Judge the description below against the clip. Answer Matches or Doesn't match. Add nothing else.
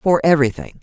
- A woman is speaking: Matches